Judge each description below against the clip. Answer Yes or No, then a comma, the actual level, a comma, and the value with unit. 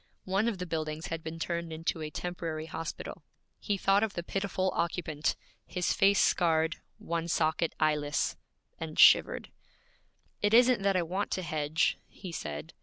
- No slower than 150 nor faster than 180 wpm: Yes, average, 160 wpm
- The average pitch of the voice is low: No, medium, 170 Hz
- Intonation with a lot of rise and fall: No, average, 3.2 semitones